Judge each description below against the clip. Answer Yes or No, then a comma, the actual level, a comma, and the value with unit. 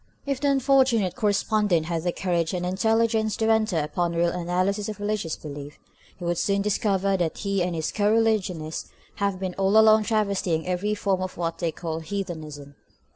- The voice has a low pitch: No, high, 190 Hz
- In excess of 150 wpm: Yes, average, 180 wpm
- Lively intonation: No, average, 3.9 semitones